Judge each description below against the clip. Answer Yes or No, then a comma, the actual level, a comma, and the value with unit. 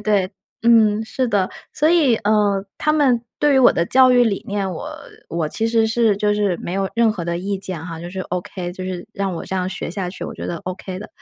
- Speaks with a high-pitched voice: Yes, high, 200 Hz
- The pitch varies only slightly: No, average, 3.7 semitones